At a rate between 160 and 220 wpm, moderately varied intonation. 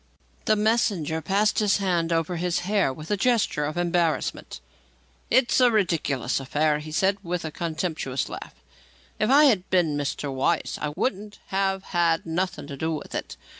Yes: average, 170 wpm; average, 4.5 semitones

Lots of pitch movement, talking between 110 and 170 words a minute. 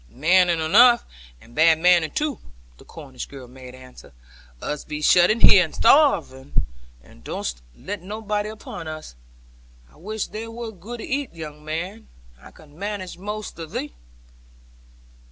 Yes: wide, 6.0 semitones; average, 155 wpm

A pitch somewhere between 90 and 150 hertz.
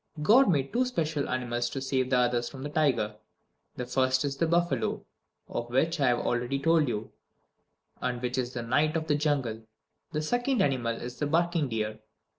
Yes: low, 135 Hz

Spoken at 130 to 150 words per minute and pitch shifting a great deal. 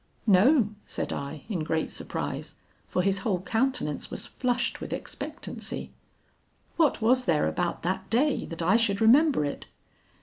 Yes: average, 145 wpm; wide, 6.4 semitones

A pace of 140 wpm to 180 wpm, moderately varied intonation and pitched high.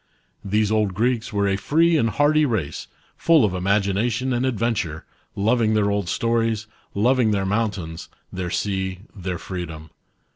No: average, 145 wpm; average, 3.6 semitones; low, 105 Hz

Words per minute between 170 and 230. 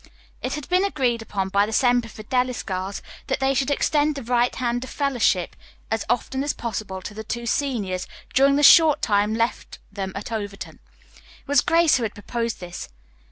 Yes: average, 190 wpm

